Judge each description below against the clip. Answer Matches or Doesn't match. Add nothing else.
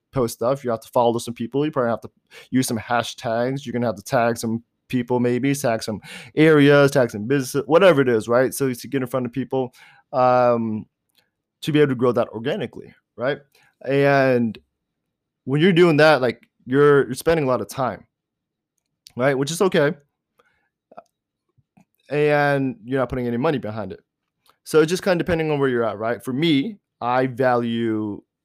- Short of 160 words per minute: Doesn't match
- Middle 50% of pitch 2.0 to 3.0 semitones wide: Doesn't match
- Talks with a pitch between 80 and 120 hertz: Doesn't match